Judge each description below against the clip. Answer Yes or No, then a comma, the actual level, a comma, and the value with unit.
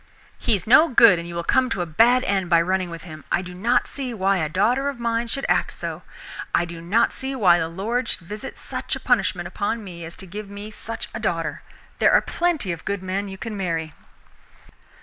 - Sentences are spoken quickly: Yes, fast, 230 wpm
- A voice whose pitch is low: No, high, 195 Hz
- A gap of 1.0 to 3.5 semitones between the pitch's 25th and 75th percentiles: No, average, 5.1 semitones